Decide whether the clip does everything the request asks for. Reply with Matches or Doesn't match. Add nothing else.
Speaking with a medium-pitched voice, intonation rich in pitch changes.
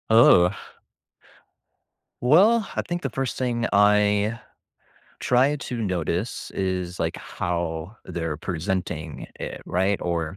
Doesn't match